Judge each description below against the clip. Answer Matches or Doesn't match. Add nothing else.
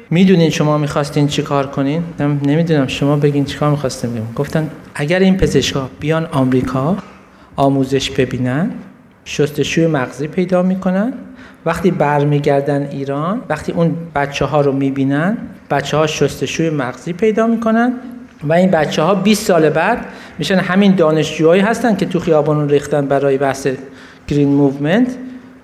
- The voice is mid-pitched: Matches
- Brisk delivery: Doesn't match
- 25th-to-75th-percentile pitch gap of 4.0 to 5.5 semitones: Matches